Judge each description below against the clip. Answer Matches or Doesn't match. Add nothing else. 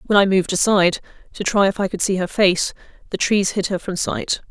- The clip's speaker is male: Doesn't match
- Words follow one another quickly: Matches